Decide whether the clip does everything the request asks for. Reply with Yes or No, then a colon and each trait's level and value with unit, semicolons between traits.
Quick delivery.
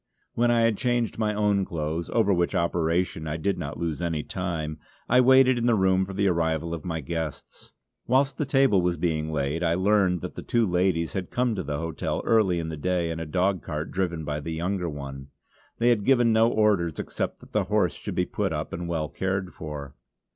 Yes: fast, 215 wpm